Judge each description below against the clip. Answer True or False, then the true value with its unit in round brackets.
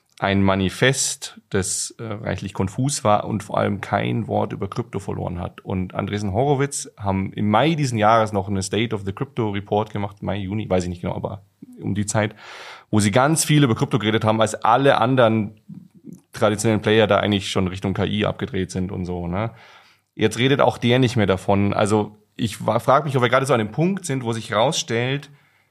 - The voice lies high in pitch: False (105 Hz)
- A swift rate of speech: True (200 wpm)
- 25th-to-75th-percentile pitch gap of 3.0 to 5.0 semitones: True (4.2 semitones)